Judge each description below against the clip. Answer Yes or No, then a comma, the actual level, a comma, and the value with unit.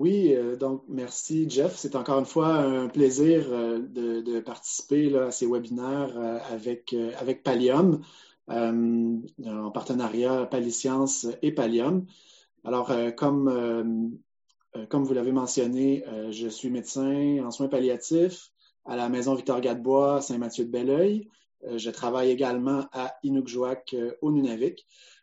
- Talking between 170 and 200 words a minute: No, average, 150 wpm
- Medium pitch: No, low, 130 Hz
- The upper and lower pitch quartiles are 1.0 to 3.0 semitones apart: Yes, narrow, 2.5 semitones